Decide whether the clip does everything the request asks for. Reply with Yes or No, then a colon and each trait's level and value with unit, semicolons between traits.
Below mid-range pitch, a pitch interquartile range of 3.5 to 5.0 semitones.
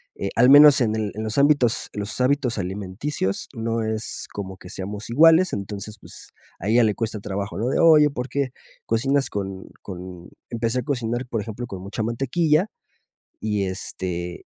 Yes: low, 110 Hz; average, 4.5 semitones